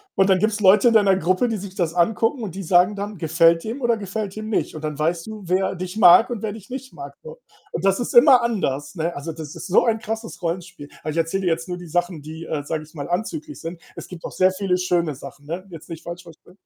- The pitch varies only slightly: No, average, 4.4 semitones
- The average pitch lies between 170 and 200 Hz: Yes, medium, 185 Hz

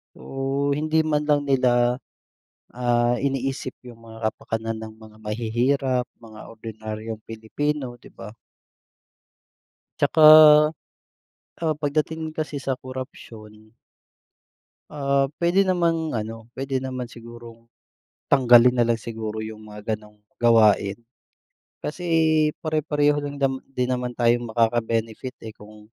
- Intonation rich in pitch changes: No, average, 4.1 semitones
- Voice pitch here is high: No, low, 120 Hz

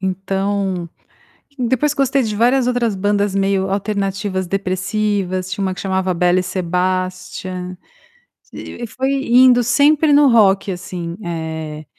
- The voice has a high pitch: Yes, high, 195 Hz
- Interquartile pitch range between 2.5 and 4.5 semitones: Yes, average, 4.1 semitones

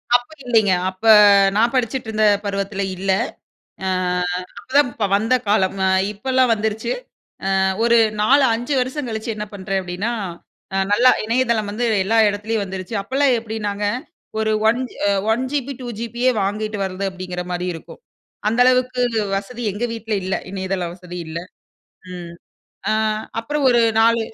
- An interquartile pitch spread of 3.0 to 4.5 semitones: Yes, average, 3.7 semitones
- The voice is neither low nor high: No, high, 220 Hz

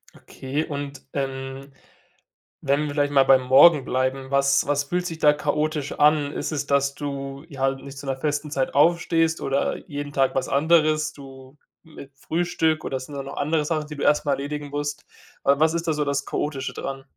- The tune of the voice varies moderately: No, narrow, 2.0 semitones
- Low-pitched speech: No, medium, 145 Hz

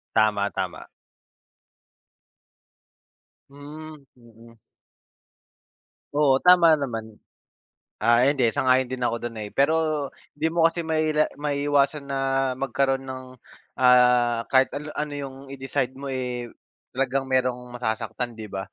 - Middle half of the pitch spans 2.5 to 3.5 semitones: Yes, average, 3.1 semitones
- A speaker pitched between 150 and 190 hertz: No, low, 130 Hz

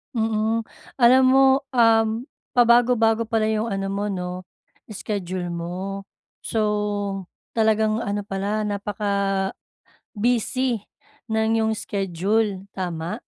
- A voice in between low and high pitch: No, high, 210 Hz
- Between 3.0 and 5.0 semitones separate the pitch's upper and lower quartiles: No, narrow, 2.4 semitones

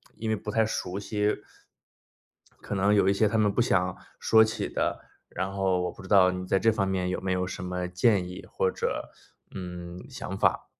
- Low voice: Yes, very low, 95 Hz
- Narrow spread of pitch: Yes, narrow, 2.3 semitones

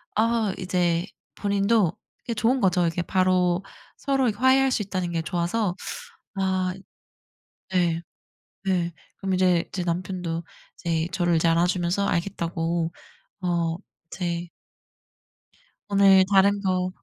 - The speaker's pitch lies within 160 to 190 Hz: Yes, medium, 185 Hz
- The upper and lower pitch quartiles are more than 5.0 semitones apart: No, narrow, 2.5 semitones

